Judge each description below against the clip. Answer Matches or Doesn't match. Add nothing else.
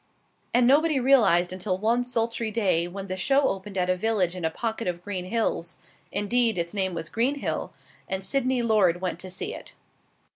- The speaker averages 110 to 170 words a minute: Doesn't match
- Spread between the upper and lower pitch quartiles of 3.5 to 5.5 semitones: Matches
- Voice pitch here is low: Doesn't match